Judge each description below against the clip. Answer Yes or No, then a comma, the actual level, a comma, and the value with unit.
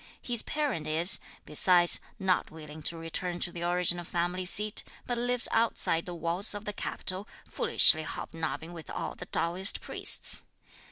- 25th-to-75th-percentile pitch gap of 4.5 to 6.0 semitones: No, average, 3.6 semitones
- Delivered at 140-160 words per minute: Yes, average, 155 wpm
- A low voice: No, medium, 175 Hz